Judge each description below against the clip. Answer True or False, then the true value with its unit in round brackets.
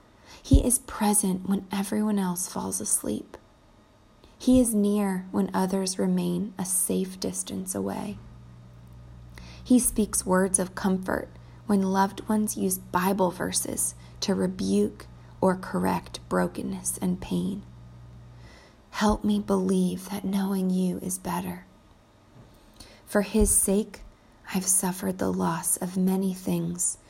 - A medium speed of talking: False (120 wpm)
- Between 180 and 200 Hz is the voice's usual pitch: True (185 Hz)